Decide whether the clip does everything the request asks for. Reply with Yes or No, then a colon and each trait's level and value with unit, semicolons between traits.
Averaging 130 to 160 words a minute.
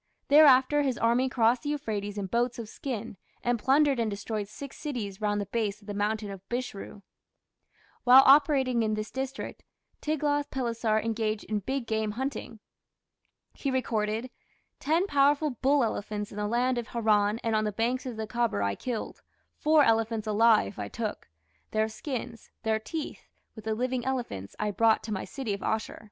No: average, 175 wpm